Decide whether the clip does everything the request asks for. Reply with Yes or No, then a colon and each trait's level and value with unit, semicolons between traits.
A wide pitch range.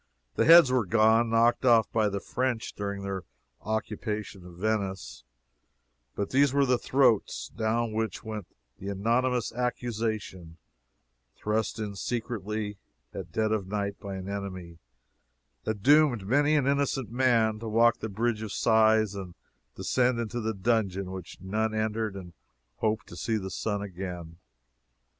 No: average, 3.0 semitones